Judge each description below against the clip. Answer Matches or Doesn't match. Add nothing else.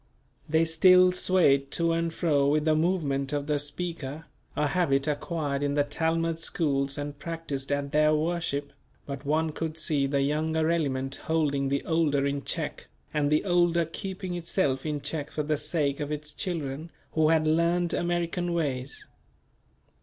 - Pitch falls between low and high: Matches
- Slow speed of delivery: Doesn't match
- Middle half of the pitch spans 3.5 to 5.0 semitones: Doesn't match